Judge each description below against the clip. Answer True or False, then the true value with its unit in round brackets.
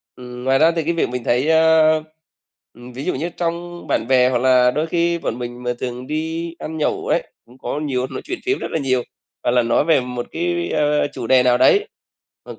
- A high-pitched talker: False (140 Hz)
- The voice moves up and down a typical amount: True (4.6 semitones)